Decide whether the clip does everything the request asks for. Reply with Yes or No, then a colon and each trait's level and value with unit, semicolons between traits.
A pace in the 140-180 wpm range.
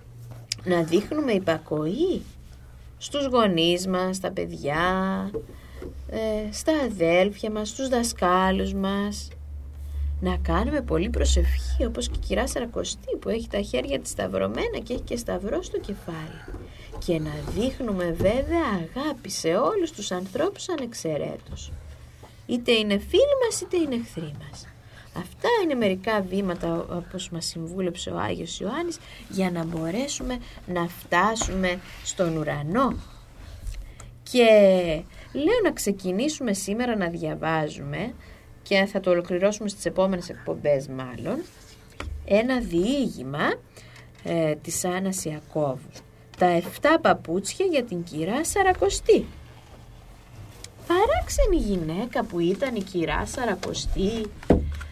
No: slow, 115 wpm